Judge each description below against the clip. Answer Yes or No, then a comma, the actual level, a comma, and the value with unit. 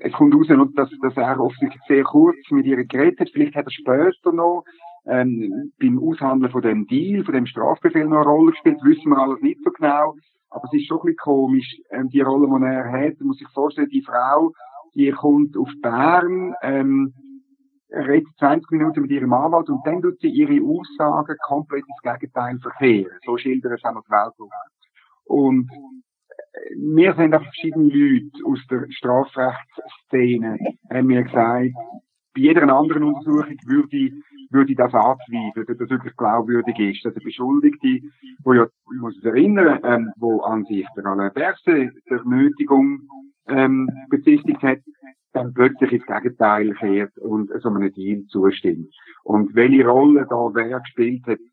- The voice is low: No, medium, 145 Hz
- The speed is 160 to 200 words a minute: Yes, average, 165 wpm